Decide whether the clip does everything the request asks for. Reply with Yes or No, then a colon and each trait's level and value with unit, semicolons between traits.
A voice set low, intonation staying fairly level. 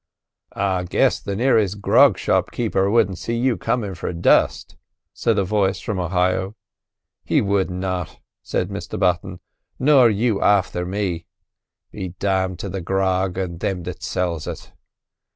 Yes: very low, 95 Hz; narrow, 2.3 semitones